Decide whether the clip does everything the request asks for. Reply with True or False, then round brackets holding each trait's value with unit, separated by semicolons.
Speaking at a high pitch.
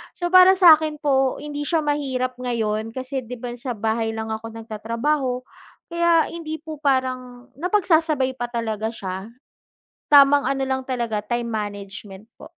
True (255 Hz)